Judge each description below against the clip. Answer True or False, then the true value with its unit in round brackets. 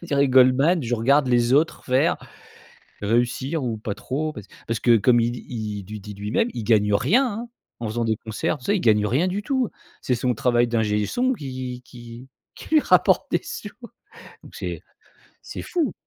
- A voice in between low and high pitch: False (125 Hz)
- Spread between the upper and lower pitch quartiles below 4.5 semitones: False (5.0 semitones)